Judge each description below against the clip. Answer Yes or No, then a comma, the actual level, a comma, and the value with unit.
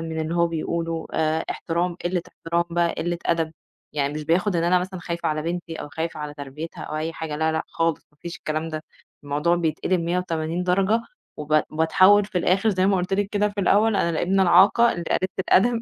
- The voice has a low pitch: No, medium, 170 Hz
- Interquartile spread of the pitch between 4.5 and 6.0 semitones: No, narrow, 2.4 semitones